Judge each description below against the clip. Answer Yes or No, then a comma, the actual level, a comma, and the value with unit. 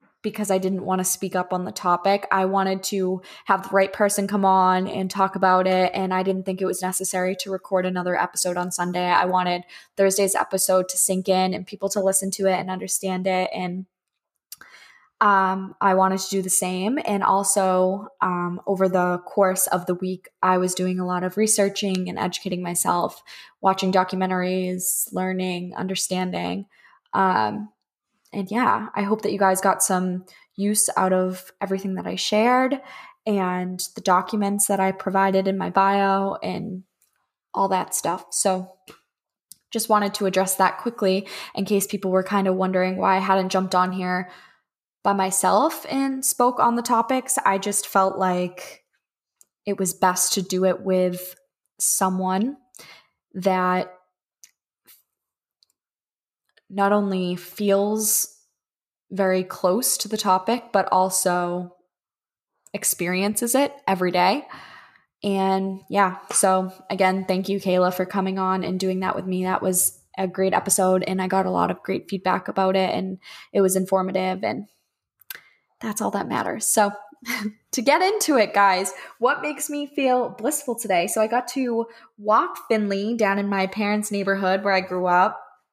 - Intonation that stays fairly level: Yes, narrow, 1.6 semitones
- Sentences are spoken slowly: No, average, 165 wpm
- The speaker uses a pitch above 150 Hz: Yes, high, 190 Hz